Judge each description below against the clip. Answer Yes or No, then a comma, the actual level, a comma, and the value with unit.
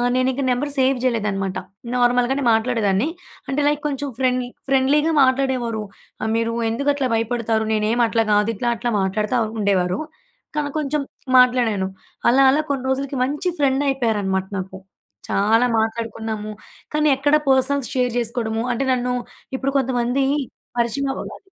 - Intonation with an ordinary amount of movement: Yes, average, 3.4 semitones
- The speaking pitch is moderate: No, high, 245 Hz